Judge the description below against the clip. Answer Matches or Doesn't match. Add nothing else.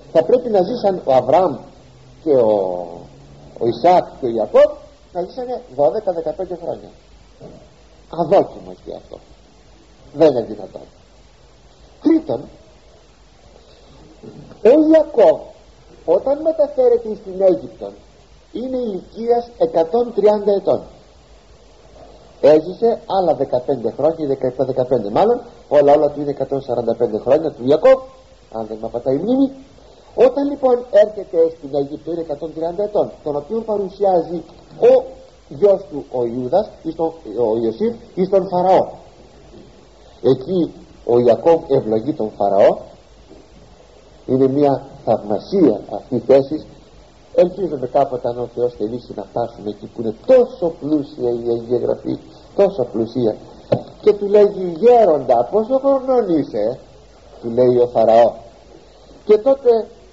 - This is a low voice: Doesn't match